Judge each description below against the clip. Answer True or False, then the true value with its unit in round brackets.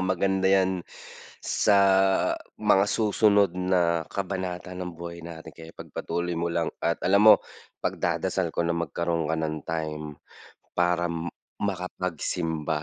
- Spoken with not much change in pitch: True (2.0 semitones)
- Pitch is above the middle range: False (85 Hz)